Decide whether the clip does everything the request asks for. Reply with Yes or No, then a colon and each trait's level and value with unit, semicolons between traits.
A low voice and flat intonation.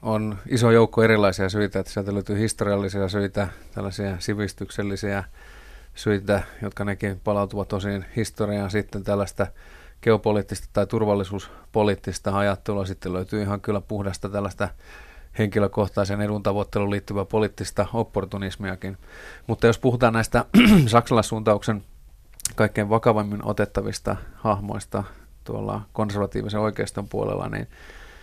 Yes: low, 105 Hz; narrow, 1.5 semitones